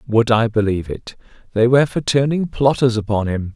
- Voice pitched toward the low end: Yes, low, 115 Hz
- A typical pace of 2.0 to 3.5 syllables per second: No, 5.6 syllables/s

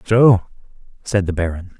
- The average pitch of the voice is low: Yes, low, 100 Hz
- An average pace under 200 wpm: Yes, slow, 135 wpm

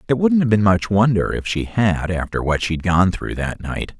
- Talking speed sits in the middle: No, fast, 240 wpm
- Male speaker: Yes, male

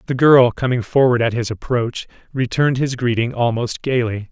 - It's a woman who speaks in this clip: No, male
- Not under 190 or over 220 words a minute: No, average, 165 wpm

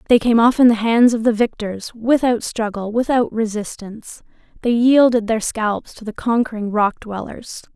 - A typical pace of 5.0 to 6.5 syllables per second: No, 4.7 syllables/s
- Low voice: No, high, 225 Hz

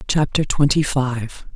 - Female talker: Yes, female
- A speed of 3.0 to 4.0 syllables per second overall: Yes, 3.6 syllables/s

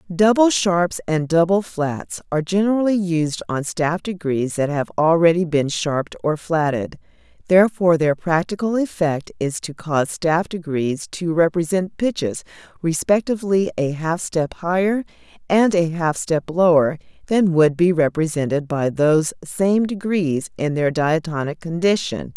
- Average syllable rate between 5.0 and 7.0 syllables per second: No, 4.5 syllables/s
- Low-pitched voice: No, medium, 170 Hz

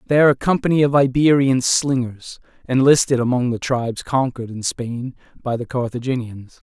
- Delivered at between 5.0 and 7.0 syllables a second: Yes, 5.4 syllables/s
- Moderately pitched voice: No, low, 130 Hz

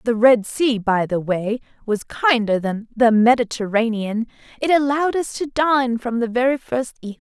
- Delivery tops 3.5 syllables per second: Yes, 4.9 syllables/s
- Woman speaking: Yes, female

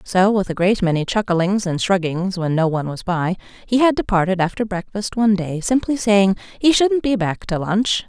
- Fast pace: Yes, fast, 210 wpm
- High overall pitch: Yes, high, 195 Hz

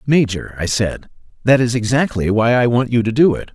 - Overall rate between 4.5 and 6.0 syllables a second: Yes, 5.3 syllables/s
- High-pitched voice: No, low, 120 Hz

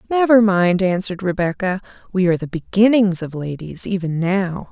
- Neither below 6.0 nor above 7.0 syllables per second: No, 5.3 syllables/s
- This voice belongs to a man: No, female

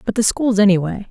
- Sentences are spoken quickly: Yes, fast, 220 wpm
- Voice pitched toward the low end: No, high, 210 Hz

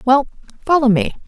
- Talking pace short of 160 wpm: Yes, average, 140 wpm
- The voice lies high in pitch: Yes, very high, 265 Hz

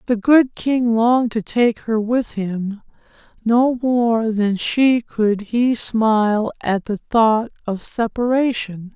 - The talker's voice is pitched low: No, high, 225 Hz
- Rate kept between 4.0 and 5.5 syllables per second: No, 3.3 syllables/s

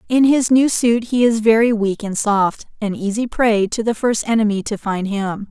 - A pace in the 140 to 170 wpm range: No, fast, 205 wpm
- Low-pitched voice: No, high, 220 Hz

